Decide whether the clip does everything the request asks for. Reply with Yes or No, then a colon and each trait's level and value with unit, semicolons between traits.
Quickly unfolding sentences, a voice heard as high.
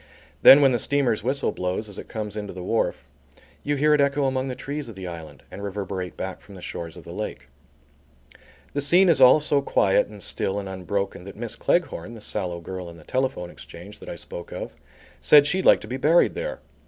No: fast, 220 wpm; low, 110 Hz